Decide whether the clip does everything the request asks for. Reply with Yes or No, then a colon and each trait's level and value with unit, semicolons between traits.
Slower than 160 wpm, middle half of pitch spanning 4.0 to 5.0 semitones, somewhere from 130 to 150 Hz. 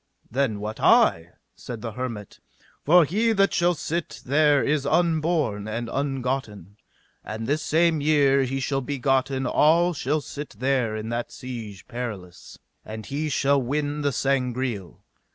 Yes: average, 150 wpm; average, 4.4 semitones; low, 135 Hz